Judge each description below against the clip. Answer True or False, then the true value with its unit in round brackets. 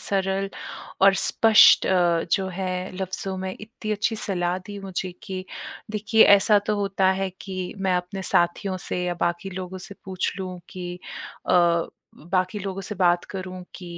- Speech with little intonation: True (1.4 semitones)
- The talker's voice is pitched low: False (190 Hz)